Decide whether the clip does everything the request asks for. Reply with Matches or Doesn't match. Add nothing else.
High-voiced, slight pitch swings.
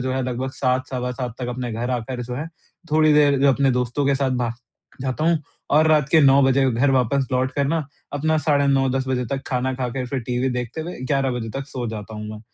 Doesn't match